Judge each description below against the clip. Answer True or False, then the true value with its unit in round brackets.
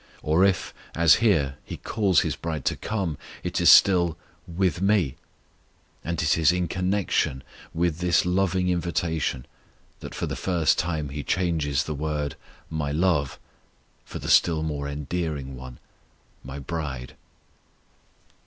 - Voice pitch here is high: False (80 Hz)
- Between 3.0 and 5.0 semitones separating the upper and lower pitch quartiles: True (3.7 semitones)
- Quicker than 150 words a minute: False (140 wpm)